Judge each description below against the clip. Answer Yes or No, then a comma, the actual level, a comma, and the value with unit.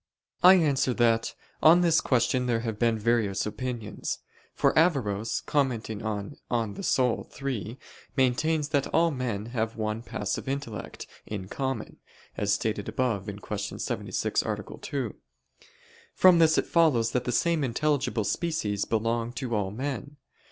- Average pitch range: Yes, average, 4.5 semitones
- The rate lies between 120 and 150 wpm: Yes, average, 140 wpm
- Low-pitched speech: Yes, low, 120 Hz